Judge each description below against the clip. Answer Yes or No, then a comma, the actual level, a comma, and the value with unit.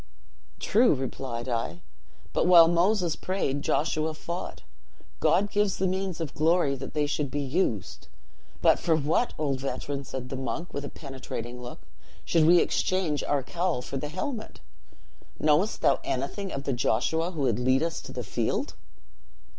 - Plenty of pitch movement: No, average, 4.8 semitones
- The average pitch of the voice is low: No, medium, 150 Hz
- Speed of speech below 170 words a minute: Yes, average, 160 wpm